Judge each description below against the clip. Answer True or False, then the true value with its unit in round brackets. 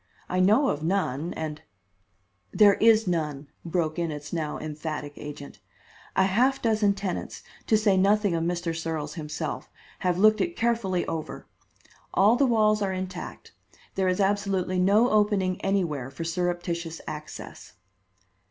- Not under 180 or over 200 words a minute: False (145 wpm)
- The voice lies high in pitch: False (180 Hz)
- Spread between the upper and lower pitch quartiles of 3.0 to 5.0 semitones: True (4.4 semitones)